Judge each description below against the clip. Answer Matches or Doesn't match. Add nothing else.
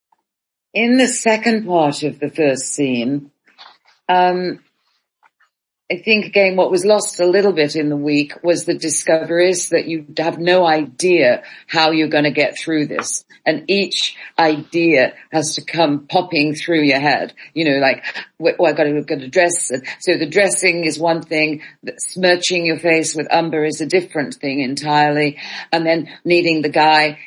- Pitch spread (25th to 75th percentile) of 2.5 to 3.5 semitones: Matches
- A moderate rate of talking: Matches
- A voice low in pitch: Doesn't match